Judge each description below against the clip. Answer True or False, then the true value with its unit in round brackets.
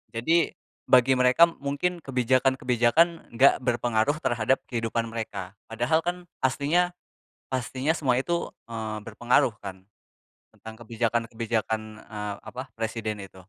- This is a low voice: True (120 Hz)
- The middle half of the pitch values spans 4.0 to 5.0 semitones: False (3.4 semitones)